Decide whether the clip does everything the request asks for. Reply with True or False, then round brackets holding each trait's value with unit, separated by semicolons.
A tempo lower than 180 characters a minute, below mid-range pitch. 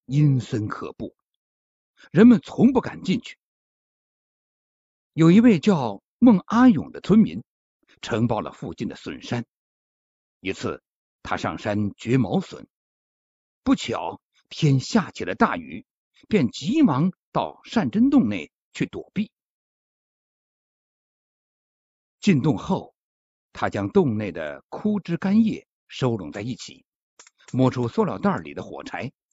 False (170 characters per minute; 185 Hz)